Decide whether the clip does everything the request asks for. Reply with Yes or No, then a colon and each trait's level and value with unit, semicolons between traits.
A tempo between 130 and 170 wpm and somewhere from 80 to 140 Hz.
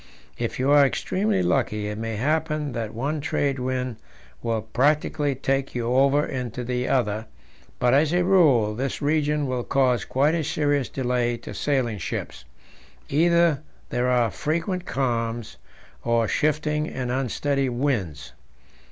Yes: average, 145 wpm; low, 135 Hz